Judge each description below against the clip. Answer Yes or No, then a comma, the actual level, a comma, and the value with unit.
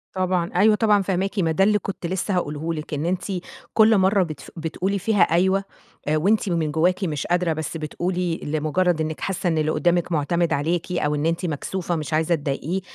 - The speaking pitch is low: No, medium, 175 Hz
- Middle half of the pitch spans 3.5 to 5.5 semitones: No, average, 3.1 semitones